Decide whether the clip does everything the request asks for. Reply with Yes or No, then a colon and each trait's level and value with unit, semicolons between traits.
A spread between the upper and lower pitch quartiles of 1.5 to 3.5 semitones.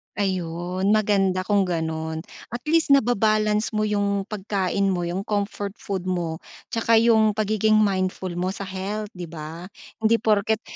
Yes: narrow, 2.6 semitones